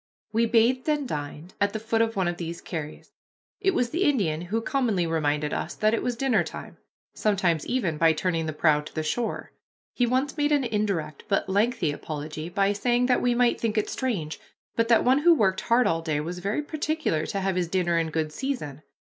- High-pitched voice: Yes, high, 200 Hz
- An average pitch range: No, wide, 7.1 semitones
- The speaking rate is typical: No, fast, 215 wpm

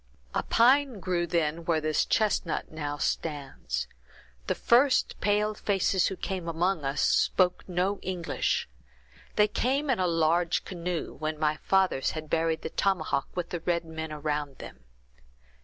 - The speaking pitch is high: No, medium, 170 Hz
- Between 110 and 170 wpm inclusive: Yes, average, 150 wpm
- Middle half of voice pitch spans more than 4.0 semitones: No, average, 3.7 semitones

